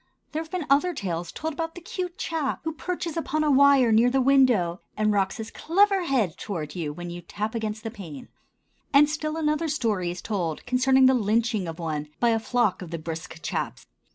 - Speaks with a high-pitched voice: Yes, high, 235 Hz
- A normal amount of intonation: No, wide, 8.8 semitones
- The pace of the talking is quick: Yes, fast, 210 wpm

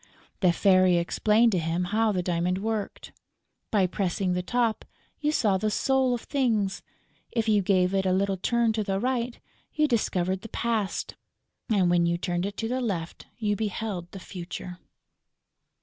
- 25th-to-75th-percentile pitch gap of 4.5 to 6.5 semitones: No, average, 3.8 semitones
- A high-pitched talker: Yes, high, 200 Hz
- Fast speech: No, average, 170 wpm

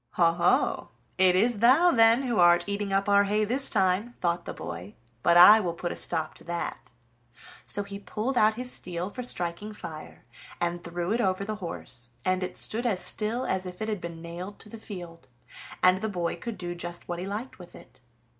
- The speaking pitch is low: No, high, 190 Hz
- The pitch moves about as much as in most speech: Yes, average, 3.8 semitones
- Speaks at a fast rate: Yes, fast, 210 wpm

